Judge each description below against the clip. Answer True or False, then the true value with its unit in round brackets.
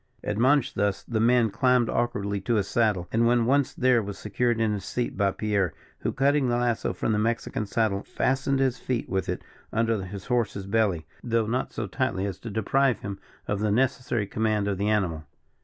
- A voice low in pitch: True (110 Hz)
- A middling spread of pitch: True (3.3 semitones)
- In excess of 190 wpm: True (200 wpm)